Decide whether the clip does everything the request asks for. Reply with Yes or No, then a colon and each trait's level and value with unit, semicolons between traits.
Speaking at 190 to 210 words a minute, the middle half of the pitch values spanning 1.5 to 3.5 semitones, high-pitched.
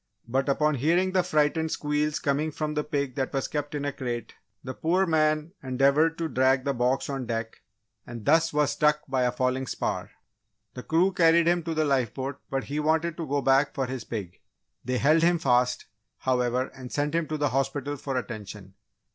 No: average, 195 wpm; average, 3.2 semitones; medium, 140 Hz